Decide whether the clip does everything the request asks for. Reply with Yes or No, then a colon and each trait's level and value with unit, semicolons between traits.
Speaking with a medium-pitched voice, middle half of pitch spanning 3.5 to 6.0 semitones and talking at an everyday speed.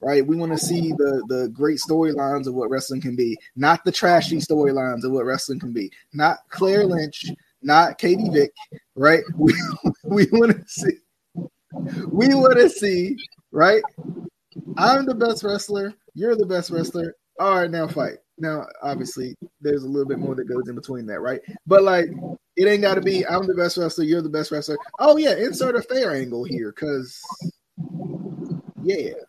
Yes: medium, 170 Hz; wide, 5.6 semitones; average, 180 wpm